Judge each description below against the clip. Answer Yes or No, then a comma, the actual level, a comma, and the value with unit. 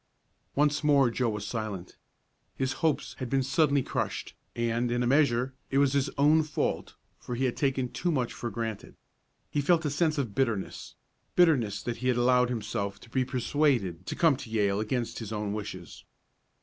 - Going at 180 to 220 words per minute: Yes, average, 185 wpm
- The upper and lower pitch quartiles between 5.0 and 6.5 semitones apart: No, average, 4.0 semitones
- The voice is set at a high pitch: No, low, 125 Hz